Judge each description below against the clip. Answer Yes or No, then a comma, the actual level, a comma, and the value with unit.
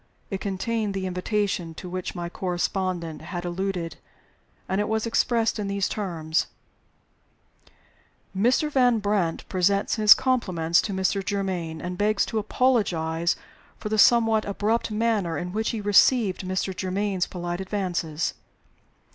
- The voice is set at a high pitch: Yes, high, 195 Hz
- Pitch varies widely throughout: No, average, 3.3 semitones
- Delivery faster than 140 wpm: No, slow, 135 wpm